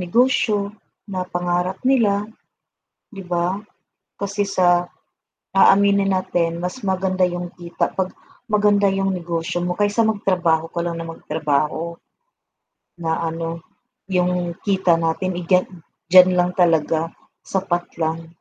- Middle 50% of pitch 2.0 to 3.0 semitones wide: Yes, narrow, 2.5 semitones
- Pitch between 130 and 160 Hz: No, medium, 180 Hz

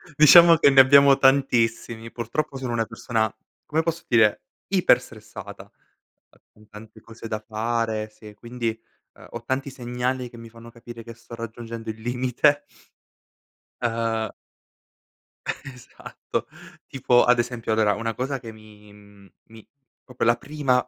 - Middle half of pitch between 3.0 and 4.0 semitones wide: No, narrow, 2.4 semitones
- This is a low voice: Yes, low, 115 Hz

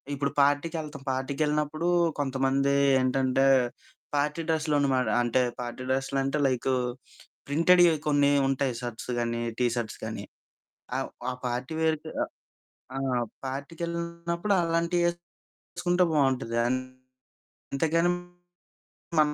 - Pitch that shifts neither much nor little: Yes, average, 3.7 semitones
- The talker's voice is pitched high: No, medium, 140 Hz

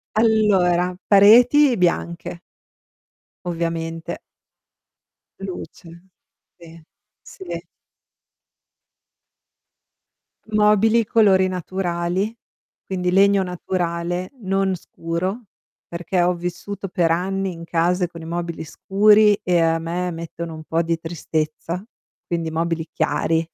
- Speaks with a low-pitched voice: No, medium, 175 Hz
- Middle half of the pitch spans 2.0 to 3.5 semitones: Yes, narrow, 2.6 semitones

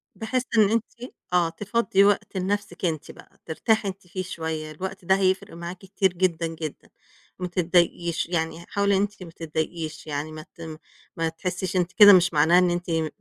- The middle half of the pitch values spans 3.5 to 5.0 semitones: No, average, 3.0 semitones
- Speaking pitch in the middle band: Yes, medium, 180 Hz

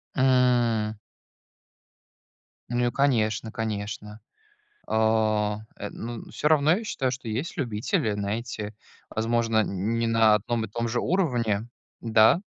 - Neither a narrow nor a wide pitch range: No, narrow, 2.2 semitones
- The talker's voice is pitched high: No, low, 115 Hz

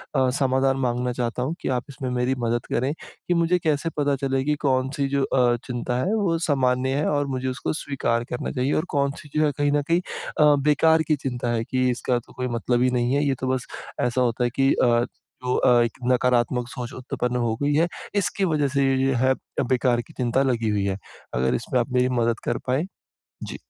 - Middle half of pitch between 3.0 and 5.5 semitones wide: No, narrow, 2.5 semitones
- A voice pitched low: Yes, low, 130 Hz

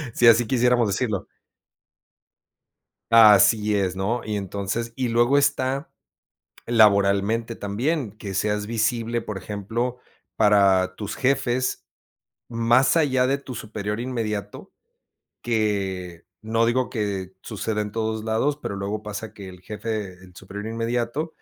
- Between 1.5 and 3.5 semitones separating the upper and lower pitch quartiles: Yes, average, 2.9 semitones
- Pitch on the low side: Yes, low, 110 Hz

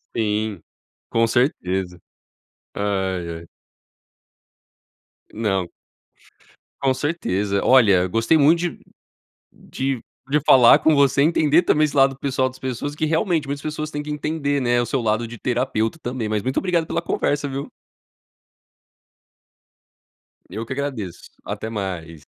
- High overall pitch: No, low, 130 Hz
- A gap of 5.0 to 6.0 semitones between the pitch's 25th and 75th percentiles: Yes, wide, 5.5 semitones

